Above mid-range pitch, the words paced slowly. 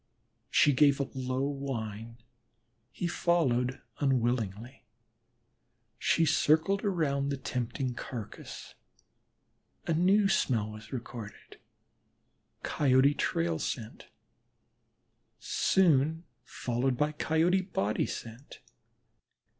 No: low, 135 Hz; slow, 85 wpm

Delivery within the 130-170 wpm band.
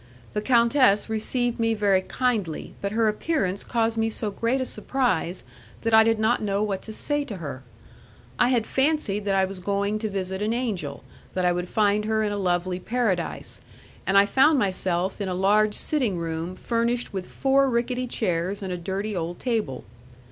No: average, 190 wpm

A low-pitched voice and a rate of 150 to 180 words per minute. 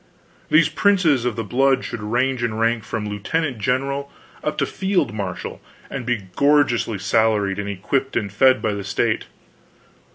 Yes: low, 120 Hz; average, 160 wpm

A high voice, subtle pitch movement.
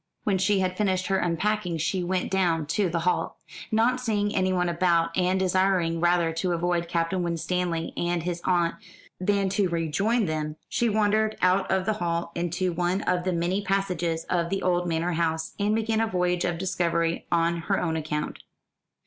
No: medium, 180 Hz; narrow, 2.3 semitones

